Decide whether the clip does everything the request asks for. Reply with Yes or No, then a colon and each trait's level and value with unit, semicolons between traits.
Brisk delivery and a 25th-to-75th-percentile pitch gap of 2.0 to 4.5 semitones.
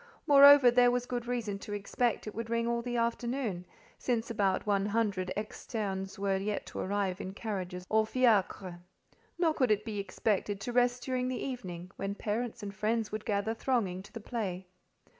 No: average, 180 wpm; average, 3.5 semitones